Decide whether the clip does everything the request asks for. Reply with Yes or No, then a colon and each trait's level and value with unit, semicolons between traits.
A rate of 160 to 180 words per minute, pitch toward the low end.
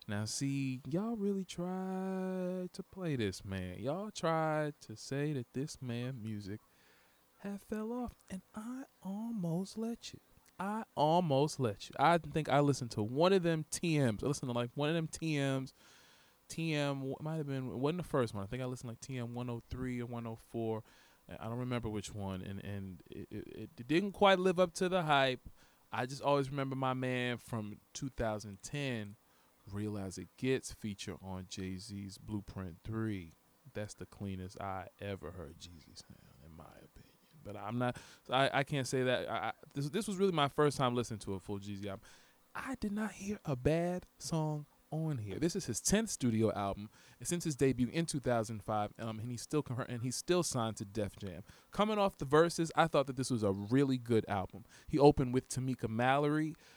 No: average, 195 wpm; low, 130 Hz